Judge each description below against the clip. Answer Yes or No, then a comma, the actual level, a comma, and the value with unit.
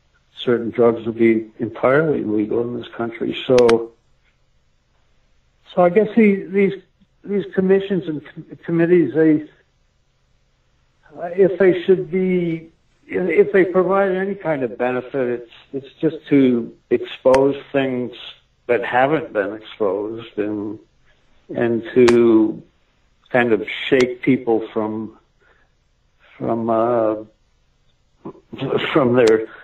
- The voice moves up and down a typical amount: No, wide, 8.2 semitones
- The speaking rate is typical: No, slow, 110 wpm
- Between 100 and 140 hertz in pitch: Yes, low, 135 Hz